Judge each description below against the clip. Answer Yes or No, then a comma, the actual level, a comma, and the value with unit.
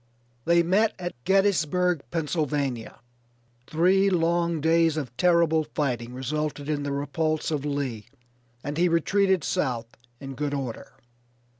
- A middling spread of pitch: Yes, average, 3.5 semitones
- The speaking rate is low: Yes, slow, 125 wpm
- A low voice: No, medium, 155 Hz